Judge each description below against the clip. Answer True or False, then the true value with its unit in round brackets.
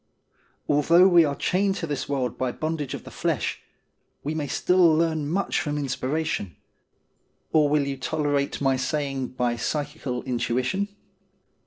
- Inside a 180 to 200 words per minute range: False (150 wpm)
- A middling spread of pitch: True (3.3 semitones)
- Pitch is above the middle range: False (145 Hz)